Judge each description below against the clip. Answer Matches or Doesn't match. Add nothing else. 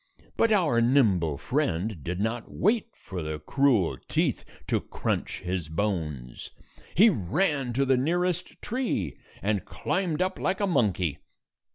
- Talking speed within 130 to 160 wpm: Matches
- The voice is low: Matches